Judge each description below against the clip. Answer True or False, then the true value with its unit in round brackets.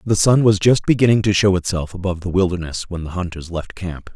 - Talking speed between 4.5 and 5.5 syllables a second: False (6.0 syllables/s)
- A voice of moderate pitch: False (95 Hz)